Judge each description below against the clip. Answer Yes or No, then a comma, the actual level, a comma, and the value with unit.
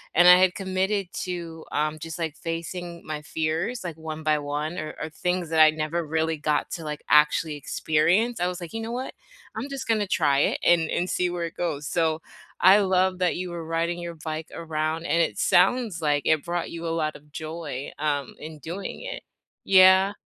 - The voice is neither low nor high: Yes, medium, 165 Hz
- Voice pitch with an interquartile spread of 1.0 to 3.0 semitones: Yes, narrow, 2.6 semitones